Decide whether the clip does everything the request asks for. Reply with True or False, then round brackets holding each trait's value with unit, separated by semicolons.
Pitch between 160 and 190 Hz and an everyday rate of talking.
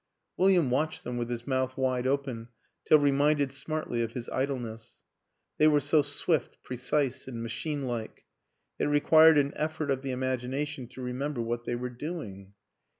False (130 Hz; 165 wpm)